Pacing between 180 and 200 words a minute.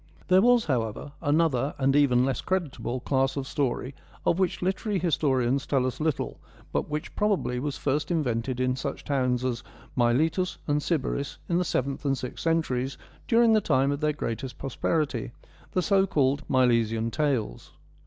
Yes: average, 185 wpm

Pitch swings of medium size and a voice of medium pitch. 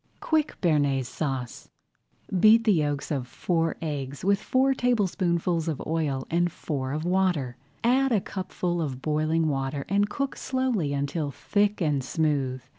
No: wide, 5.9 semitones; medium, 160 Hz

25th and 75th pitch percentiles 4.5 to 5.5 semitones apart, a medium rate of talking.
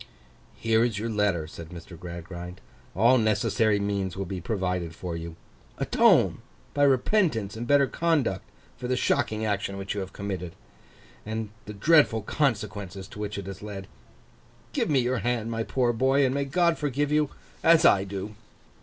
Yes: average, 5.0 semitones; average, 165 wpm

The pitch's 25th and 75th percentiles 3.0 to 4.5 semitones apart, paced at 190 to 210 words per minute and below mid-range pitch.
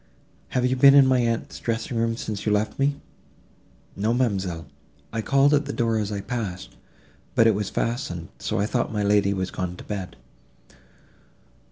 No: average, 3.7 semitones; average, 180 wpm; low, 110 Hz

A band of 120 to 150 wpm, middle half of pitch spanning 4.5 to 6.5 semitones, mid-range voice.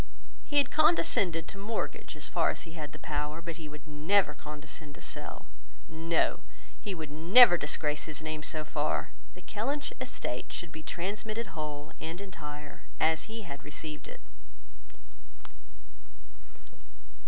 Yes: average, 145 wpm; average, 4.8 semitones; medium, 160 Hz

